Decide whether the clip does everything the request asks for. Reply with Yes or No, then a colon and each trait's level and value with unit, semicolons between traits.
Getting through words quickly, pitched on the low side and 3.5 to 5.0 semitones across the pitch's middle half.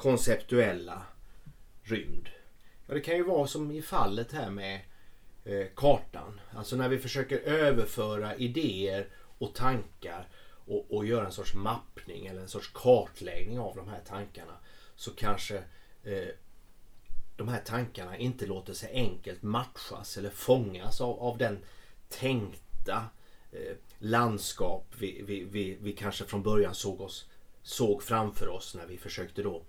No: average, 145 wpm; low, 100 Hz; average, 3.8 semitones